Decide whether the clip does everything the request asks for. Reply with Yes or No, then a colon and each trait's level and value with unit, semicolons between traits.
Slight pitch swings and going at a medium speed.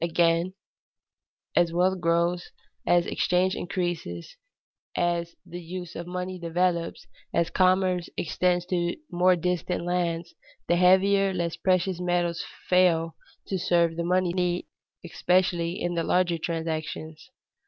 No: narrow, 1.3 semitones; slow, 120 wpm